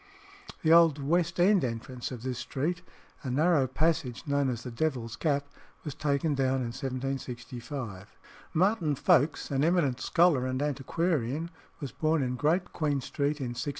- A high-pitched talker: No, medium, 140 Hz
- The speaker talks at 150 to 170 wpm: Yes, average, 155 wpm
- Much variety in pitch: No, average, 3.9 semitones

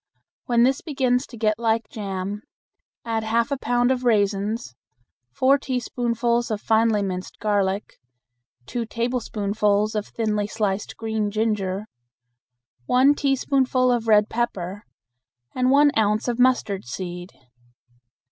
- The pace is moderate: No, slow, 120 wpm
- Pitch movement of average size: Yes, average, 3.1 semitones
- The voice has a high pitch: Yes, high, 225 Hz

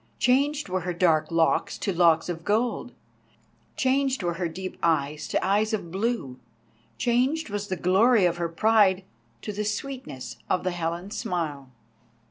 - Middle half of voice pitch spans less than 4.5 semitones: No, average, 5.1 semitones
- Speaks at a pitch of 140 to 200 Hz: Yes, high, 190 Hz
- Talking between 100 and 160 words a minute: Yes, average, 155 wpm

